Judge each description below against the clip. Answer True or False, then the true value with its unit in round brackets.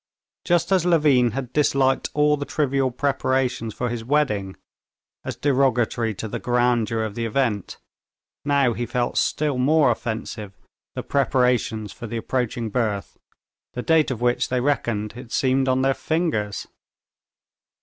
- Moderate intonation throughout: True (3.3 semitones)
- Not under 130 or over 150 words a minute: True (145 wpm)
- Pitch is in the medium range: False (125 Hz)